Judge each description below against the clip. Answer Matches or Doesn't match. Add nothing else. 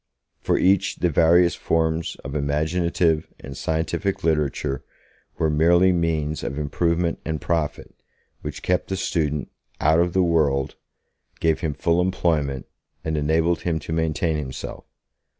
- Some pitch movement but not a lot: Doesn't match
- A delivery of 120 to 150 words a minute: Matches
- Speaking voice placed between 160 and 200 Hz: Doesn't match